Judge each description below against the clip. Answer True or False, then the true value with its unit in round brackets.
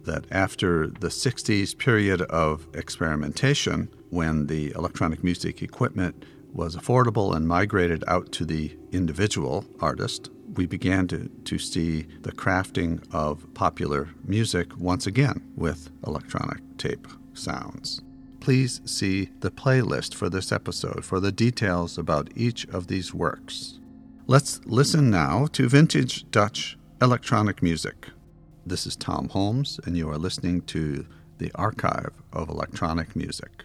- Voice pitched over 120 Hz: False (95 Hz)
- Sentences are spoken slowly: True (130 wpm)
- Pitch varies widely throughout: True (7.0 semitones)